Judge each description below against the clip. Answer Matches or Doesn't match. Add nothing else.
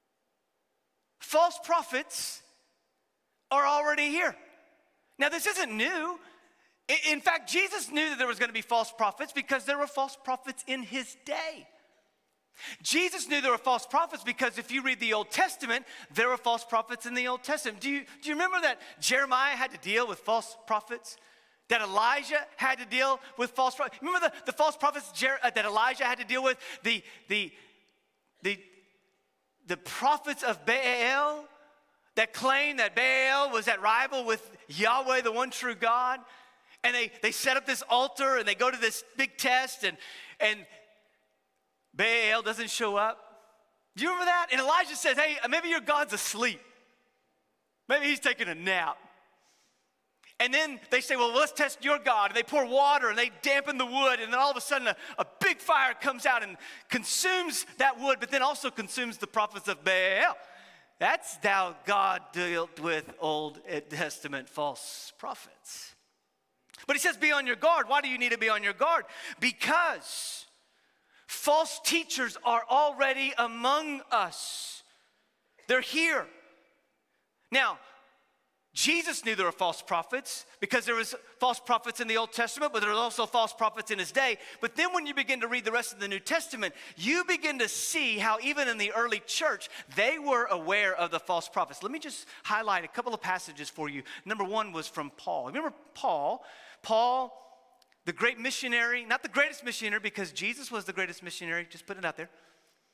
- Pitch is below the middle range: Doesn't match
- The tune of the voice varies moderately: Matches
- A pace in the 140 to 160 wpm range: Doesn't match